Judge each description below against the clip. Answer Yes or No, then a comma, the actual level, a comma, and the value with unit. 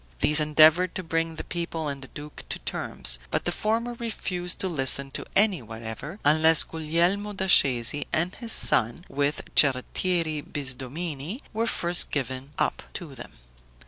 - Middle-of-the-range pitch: Yes, medium, 160 Hz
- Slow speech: No, average, 155 wpm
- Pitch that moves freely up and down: No, average, 4.7 semitones